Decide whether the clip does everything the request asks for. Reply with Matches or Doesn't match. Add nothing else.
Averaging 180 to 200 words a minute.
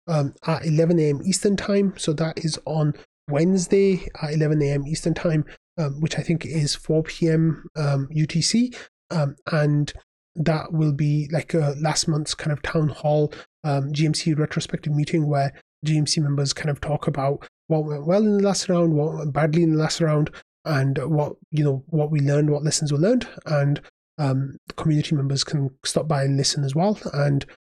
Matches